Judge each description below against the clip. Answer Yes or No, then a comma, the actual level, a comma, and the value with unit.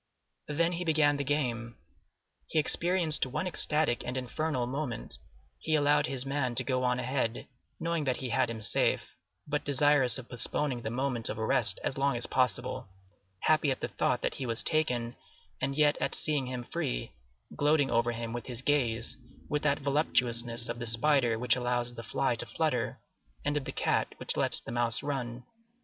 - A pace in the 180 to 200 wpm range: Yes, average, 185 wpm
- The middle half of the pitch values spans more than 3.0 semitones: Yes, average, 3.5 semitones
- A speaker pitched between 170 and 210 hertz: No, low, 130 Hz